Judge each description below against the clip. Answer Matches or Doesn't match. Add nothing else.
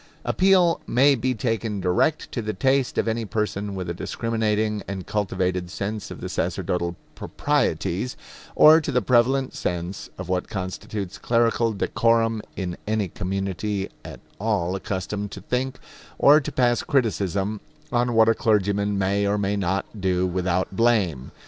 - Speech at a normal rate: Matches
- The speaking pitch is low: Matches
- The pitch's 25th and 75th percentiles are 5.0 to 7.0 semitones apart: Doesn't match